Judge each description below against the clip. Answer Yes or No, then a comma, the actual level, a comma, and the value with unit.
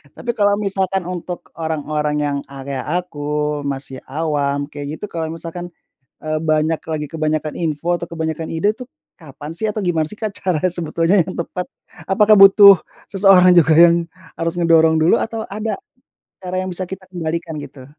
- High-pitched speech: No, medium, 165 Hz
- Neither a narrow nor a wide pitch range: Yes, average, 3.4 semitones